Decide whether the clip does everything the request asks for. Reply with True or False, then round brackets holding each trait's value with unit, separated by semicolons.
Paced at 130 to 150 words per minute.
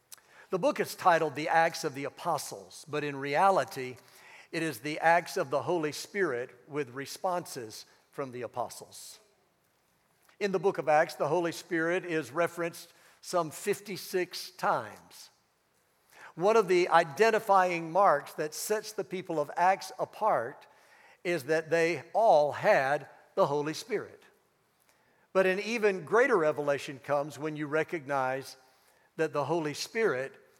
True (140 wpm)